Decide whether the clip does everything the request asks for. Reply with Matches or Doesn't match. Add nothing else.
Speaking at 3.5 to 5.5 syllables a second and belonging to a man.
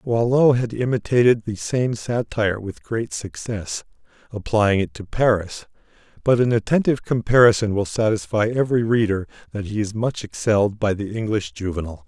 Matches